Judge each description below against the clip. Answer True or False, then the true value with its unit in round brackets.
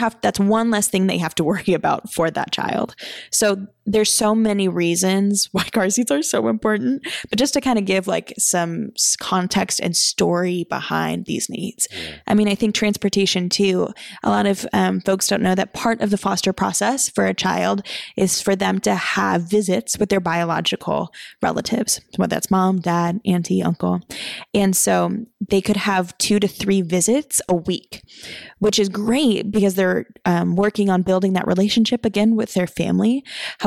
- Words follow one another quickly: False (185 wpm)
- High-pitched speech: True (195 Hz)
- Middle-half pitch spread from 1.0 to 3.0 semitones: True (2.7 semitones)